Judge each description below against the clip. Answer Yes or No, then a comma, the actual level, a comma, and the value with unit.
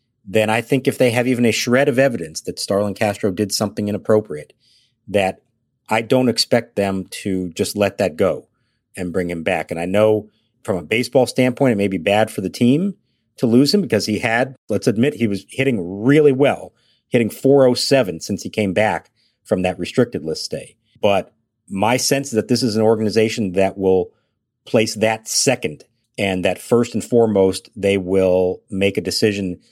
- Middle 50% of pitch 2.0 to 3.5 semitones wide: No, average, 4.1 semitones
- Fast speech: No, average, 190 wpm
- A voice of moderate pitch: No, low, 110 Hz